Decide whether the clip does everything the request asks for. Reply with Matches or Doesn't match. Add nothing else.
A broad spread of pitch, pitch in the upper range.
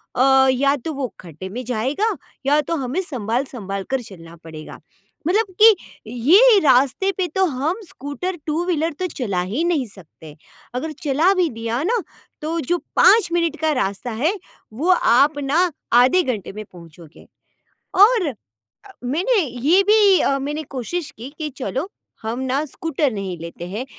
Matches